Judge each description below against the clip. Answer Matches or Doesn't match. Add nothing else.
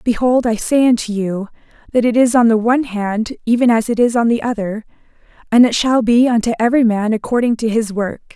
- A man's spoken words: Doesn't match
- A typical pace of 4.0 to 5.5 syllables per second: Doesn't match